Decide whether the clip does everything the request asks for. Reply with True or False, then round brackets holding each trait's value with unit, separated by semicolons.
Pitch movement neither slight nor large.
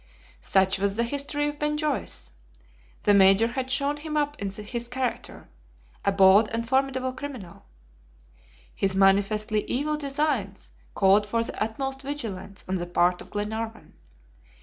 False (5.8 semitones)